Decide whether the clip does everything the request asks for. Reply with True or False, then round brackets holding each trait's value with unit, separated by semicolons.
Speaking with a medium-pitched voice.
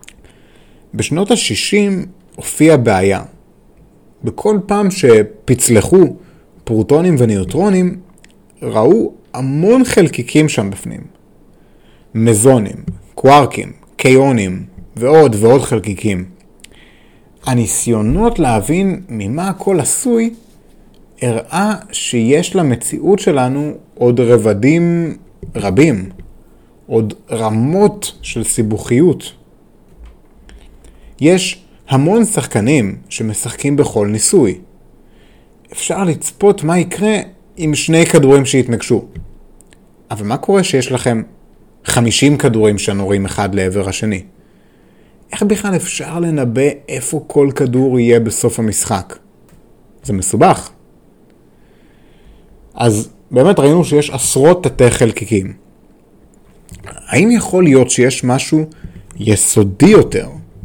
False (130 Hz)